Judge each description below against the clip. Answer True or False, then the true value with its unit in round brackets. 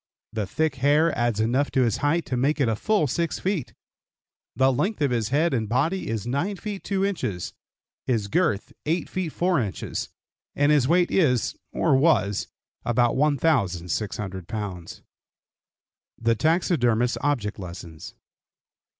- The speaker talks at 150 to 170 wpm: False (140 wpm)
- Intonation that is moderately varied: False (6.5 semitones)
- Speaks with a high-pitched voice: False (130 Hz)